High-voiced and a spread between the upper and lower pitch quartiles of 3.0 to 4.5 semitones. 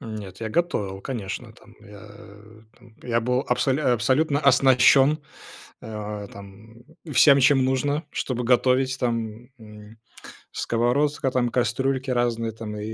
No: low, 120 Hz; average, 3.5 semitones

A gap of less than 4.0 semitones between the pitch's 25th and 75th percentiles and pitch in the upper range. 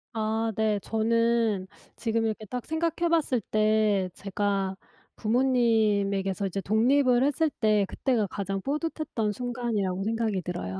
Yes: average, 3.5 semitones; high, 220 Hz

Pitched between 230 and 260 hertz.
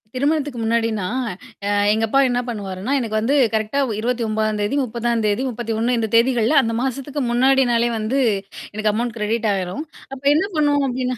Yes: high, 235 Hz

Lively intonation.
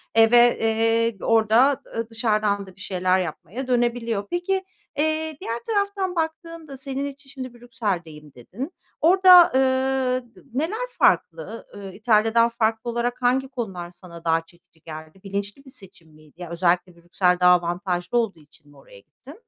Yes: wide, 6.7 semitones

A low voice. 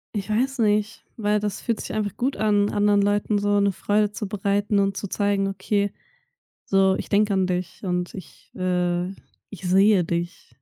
No: high, 205 Hz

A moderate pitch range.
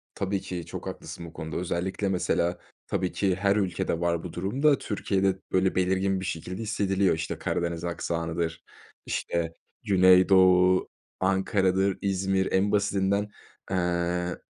No: narrow, 2.0 semitones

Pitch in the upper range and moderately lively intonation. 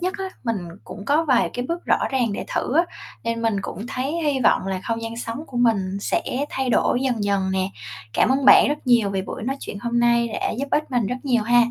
Yes: high, 240 Hz; average, 3.6 semitones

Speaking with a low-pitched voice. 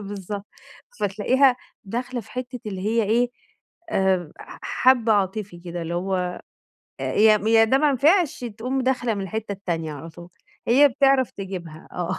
No: high, 210 Hz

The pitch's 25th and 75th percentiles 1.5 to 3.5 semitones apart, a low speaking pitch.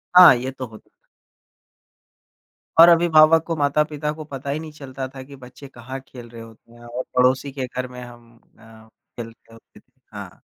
No: average, 3.9 semitones; low, 130 Hz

